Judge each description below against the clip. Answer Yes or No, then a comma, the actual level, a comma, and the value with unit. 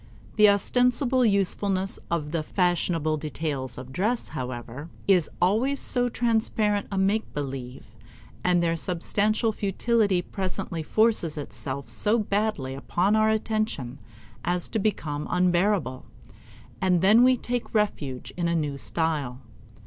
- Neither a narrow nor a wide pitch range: No, wide, 6.0 semitones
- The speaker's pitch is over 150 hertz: Yes, medium, 185 Hz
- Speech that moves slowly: Yes, slow, 125 wpm